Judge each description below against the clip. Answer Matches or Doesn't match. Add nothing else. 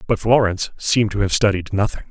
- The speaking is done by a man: Matches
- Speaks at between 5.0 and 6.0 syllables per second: Doesn't match